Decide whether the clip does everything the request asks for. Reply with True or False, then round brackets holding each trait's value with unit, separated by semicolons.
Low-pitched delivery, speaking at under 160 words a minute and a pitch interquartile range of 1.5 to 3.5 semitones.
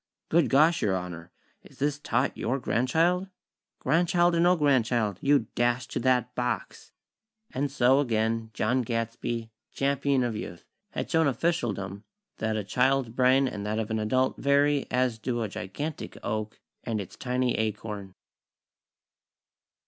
False (125 Hz; 145 wpm; 4.2 semitones)